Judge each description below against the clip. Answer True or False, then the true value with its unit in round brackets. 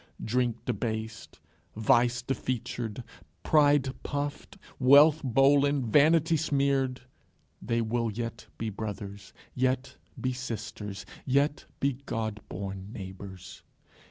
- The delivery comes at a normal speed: False (100 wpm)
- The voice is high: False (125 Hz)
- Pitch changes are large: False (4.1 semitones)